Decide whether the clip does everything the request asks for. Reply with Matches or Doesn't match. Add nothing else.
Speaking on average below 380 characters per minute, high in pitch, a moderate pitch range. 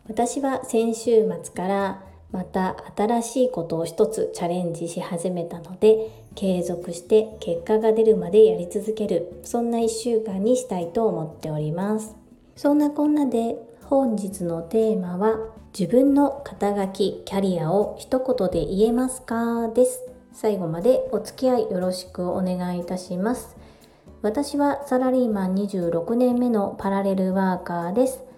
Matches